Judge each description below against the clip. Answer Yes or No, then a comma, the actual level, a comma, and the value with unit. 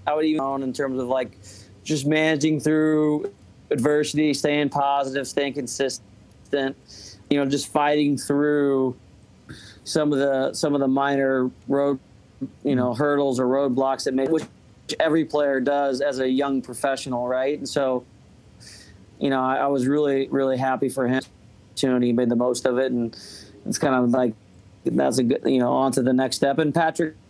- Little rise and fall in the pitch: Yes, narrow, 2.3 semitones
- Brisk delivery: No, average, 180 wpm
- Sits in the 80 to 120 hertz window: No, low, 135 Hz